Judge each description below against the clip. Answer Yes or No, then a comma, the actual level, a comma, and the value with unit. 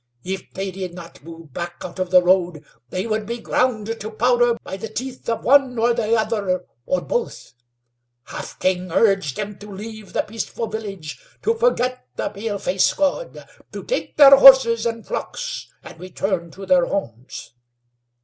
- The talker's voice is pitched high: Yes, high, 210 Hz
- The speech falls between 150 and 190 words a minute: Yes, average, 170 wpm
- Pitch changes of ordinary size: Yes, average, 4.3 semitones